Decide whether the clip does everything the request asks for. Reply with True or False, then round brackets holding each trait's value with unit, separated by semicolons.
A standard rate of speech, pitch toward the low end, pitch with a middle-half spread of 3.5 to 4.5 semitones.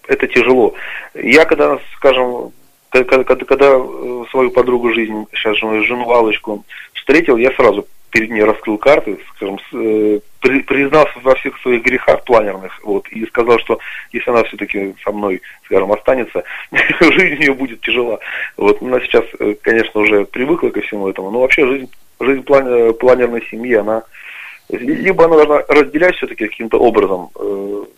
True (145 wpm; 120 Hz; 4.2 semitones)